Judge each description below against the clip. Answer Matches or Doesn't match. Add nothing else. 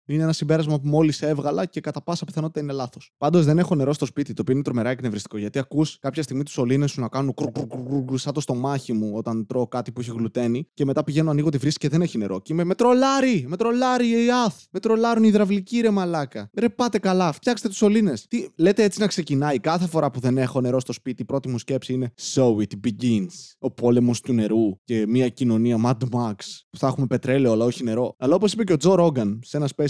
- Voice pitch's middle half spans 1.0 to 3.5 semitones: Doesn't match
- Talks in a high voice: Doesn't match